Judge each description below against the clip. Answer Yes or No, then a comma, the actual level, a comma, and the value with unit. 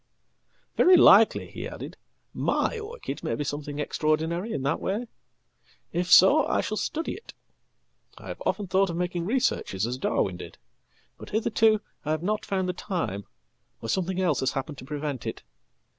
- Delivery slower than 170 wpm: Yes, average, 160 wpm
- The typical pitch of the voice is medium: Yes, medium, 180 Hz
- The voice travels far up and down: Yes, wide, 6.5 semitones